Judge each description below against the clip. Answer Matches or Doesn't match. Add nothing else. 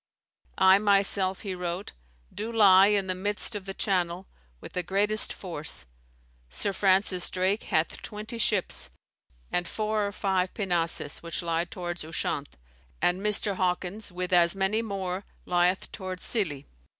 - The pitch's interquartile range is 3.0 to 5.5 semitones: Doesn't match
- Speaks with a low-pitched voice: Doesn't match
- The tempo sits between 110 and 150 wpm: Matches